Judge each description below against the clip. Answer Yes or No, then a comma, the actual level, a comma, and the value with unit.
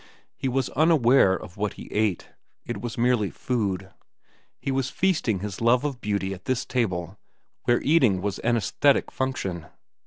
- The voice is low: Yes, low, 115 Hz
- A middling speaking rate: Yes, average, 160 wpm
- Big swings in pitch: No, average, 4.9 semitones